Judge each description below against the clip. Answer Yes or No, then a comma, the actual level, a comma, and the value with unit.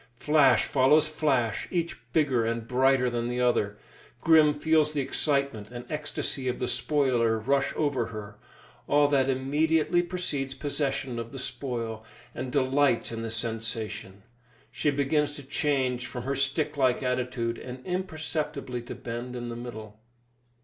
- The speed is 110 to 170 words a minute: Yes, average, 150 wpm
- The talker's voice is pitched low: Yes, low, 130 Hz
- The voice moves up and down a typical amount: Yes, average, 3.6 semitones